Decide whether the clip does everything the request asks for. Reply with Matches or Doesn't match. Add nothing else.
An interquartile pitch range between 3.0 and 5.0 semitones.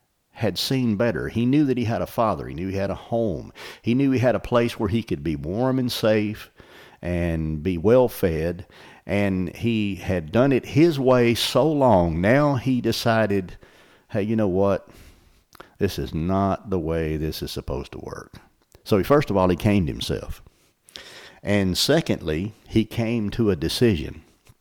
Matches